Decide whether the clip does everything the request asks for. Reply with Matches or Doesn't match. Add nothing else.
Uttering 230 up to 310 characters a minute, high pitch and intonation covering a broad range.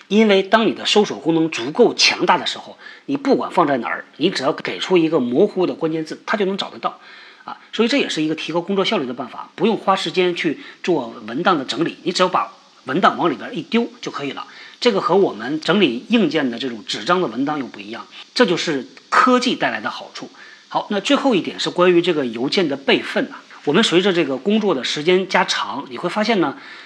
Doesn't match